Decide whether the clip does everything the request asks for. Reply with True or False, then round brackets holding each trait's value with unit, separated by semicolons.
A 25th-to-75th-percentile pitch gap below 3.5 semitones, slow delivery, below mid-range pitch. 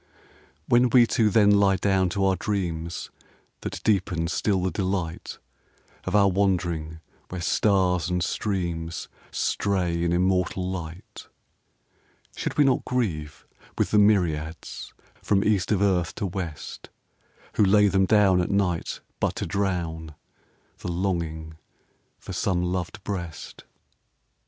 True (2.9 semitones; 130 wpm; 95 Hz)